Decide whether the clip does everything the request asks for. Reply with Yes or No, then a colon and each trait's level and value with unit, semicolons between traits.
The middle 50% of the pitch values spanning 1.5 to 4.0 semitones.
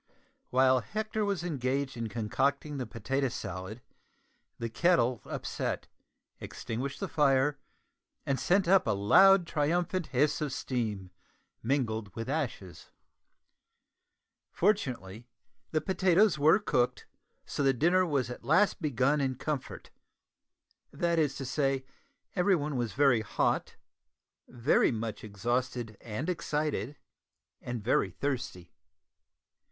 No: average, 4.8 semitones